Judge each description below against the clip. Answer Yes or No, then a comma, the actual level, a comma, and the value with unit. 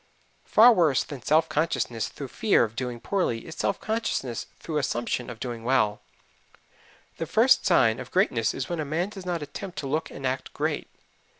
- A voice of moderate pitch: Yes, medium, 145 Hz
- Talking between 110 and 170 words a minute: No, average, 185 wpm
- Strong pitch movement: Yes, wide, 6.5 semitones